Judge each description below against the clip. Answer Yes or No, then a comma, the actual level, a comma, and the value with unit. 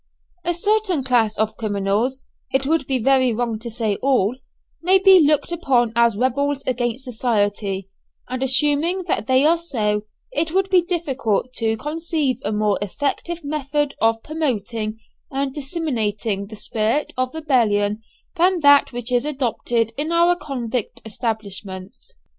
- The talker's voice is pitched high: Yes, very high, 255 Hz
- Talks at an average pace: Yes, average, 145 wpm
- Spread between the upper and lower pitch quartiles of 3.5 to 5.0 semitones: No, wide, 5.4 semitones